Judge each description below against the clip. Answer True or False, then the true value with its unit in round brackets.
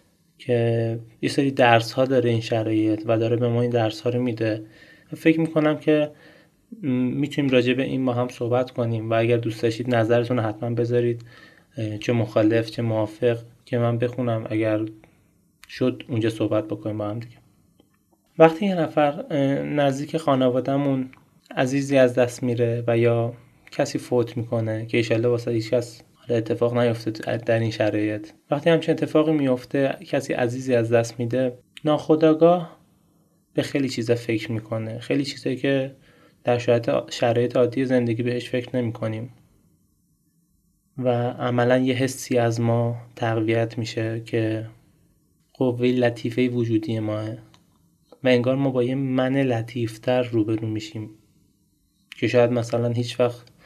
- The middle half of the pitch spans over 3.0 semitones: False (2.7 semitones)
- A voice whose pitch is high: False (120 Hz)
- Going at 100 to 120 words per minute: False (140 wpm)